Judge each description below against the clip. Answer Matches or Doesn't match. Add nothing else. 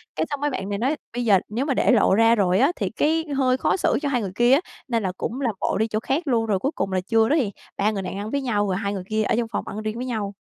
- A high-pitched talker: Matches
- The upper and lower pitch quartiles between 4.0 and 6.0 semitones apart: Matches